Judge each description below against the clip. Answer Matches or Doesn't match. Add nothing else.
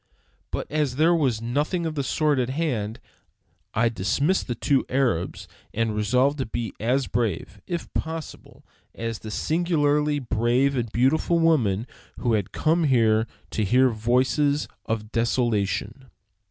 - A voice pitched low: Matches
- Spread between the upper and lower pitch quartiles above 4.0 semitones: Matches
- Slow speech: Doesn't match